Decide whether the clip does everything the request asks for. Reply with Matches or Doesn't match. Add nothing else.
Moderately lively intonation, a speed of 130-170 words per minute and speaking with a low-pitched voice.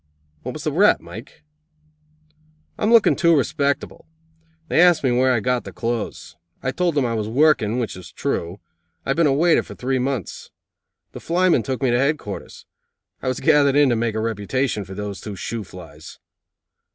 Doesn't match